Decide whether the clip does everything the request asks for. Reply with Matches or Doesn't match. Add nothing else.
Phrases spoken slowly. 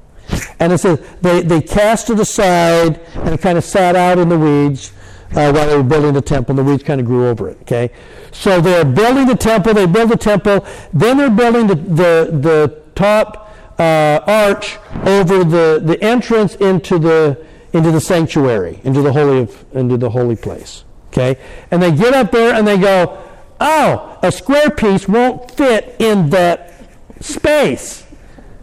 Doesn't match